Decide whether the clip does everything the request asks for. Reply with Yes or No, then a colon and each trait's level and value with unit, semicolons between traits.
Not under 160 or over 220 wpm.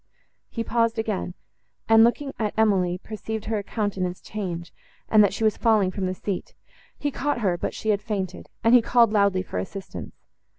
Yes: average, 180 wpm